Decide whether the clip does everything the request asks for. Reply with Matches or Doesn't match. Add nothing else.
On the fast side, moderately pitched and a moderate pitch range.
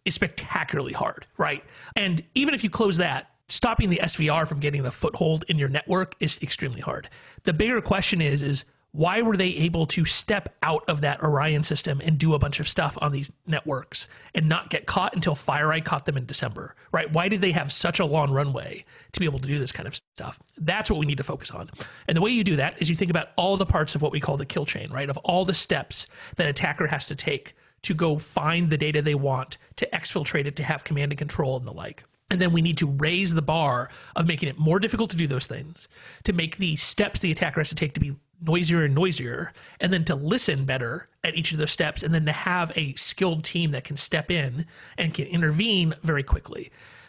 Matches